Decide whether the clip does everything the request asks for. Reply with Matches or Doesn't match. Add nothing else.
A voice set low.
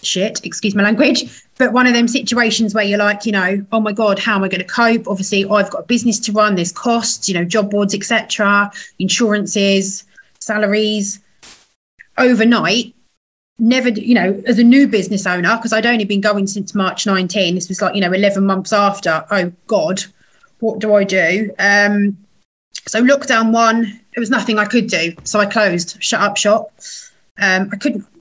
Doesn't match